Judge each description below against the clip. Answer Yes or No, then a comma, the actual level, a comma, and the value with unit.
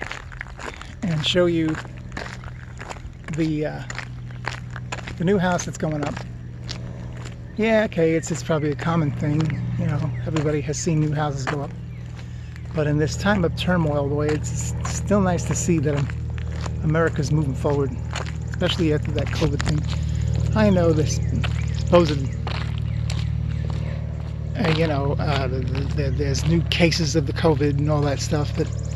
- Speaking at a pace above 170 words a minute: No, average, 150 wpm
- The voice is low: No, medium, 145 Hz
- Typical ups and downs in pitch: Yes, average, 4.7 semitones